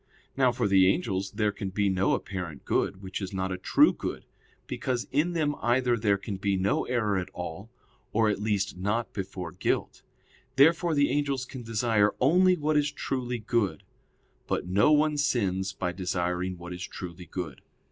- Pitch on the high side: No, low, 105 Hz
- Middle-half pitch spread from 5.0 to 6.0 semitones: Yes, average, 5.3 semitones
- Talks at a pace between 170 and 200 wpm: Yes, average, 180 wpm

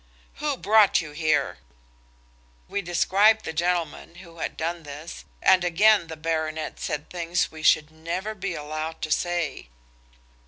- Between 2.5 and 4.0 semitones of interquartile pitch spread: Yes, average, 3.0 semitones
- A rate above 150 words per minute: No, average, 145 wpm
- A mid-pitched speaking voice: Yes, medium, 170 Hz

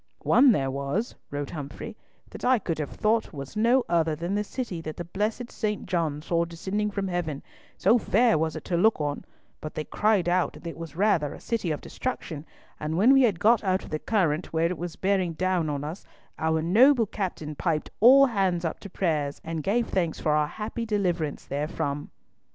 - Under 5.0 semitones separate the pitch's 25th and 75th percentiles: No, average, 5.3 semitones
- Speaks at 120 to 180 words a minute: No, fast, 205 wpm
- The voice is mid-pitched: Yes, medium, 175 Hz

